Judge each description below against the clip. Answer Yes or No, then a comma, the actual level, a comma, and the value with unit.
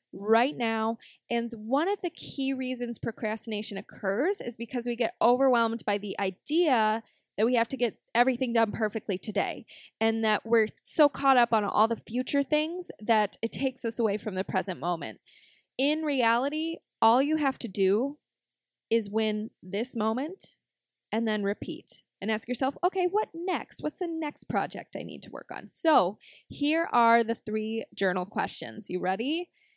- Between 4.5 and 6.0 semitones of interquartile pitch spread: No, average, 4.1 semitones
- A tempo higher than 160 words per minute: Yes, average, 170 wpm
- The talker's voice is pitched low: No, high, 230 Hz